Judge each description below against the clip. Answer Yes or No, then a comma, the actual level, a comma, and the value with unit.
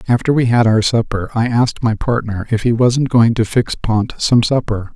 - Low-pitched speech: Yes, low, 115 Hz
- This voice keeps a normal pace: No, fast, 220 wpm